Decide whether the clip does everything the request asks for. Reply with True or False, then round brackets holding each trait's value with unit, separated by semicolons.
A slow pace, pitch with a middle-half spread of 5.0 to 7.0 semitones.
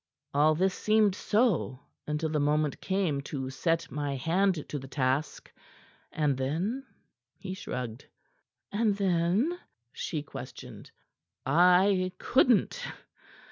True (115 wpm; 5.4 semitones)